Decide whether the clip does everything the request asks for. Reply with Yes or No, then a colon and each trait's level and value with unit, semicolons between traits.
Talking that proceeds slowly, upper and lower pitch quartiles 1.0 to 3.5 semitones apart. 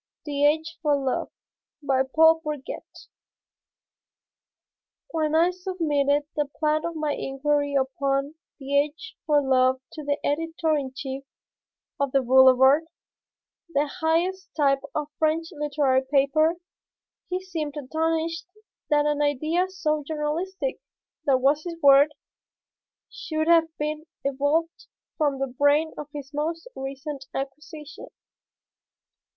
Yes: slow, 120 wpm; narrow, 2.6 semitones